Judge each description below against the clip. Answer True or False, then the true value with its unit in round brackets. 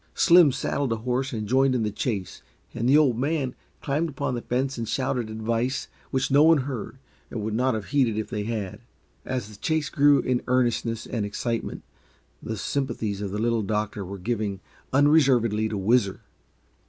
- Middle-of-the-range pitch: False (120 Hz)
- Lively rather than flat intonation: False (3.7 semitones)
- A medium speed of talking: True (180 wpm)